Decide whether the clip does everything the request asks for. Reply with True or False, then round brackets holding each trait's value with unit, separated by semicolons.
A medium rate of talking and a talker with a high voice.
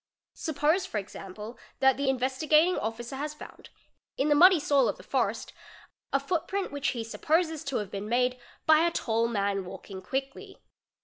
True (175 wpm; 270 Hz)